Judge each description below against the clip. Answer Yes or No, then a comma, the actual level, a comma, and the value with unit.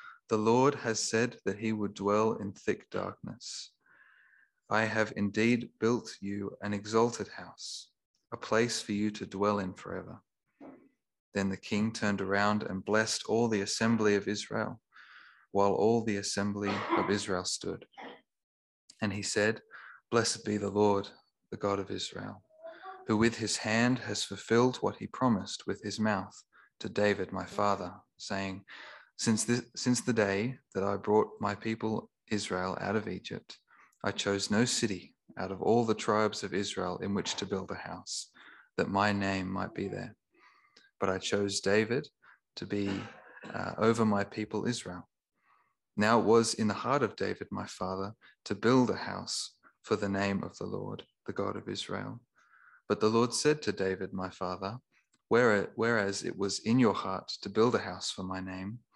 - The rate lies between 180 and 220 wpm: No, average, 170 wpm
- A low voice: Yes, low, 105 Hz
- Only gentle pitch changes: Yes, narrow, 2.3 semitones